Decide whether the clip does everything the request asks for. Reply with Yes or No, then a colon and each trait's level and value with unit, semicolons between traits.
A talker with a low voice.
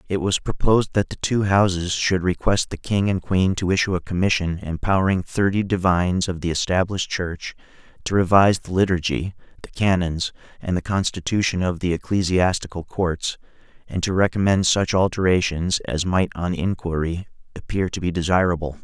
Yes: very low, 90 Hz